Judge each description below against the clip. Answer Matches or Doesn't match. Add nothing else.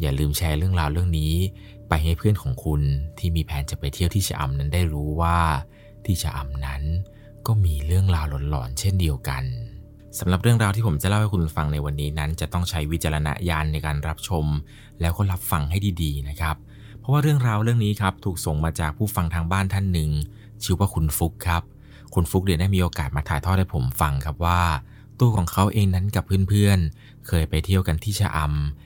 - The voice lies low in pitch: Matches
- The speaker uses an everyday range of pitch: Matches